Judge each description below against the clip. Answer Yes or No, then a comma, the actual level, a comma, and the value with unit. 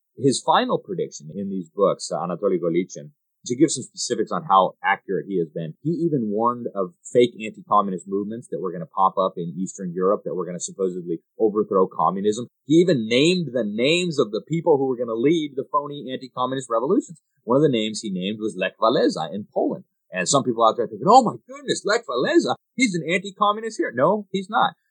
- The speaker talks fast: Yes, fast, 210 wpm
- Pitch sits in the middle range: No, low, 125 Hz